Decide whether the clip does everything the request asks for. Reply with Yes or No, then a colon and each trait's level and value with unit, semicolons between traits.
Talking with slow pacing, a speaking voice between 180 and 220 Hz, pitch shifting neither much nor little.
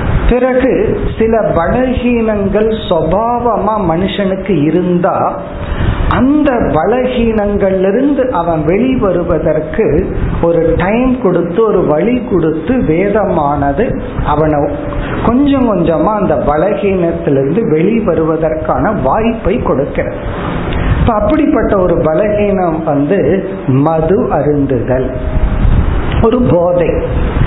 No: slow, 70 wpm; medium, 185 Hz; wide, 5.9 semitones